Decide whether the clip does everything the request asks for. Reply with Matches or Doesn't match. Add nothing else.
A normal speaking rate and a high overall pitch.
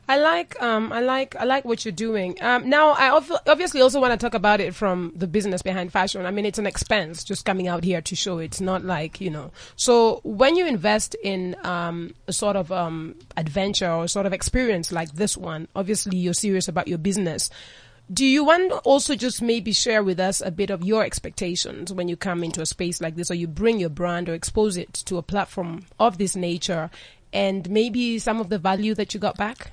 Doesn't match